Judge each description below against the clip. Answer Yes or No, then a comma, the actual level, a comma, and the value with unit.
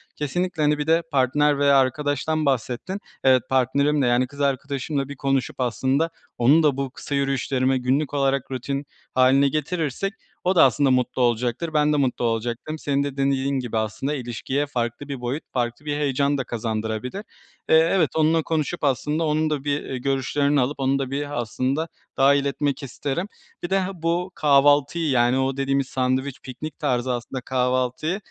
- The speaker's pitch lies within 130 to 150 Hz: Yes, medium, 140 Hz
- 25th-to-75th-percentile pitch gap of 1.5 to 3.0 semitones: Yes, narrow, 2.5 semitones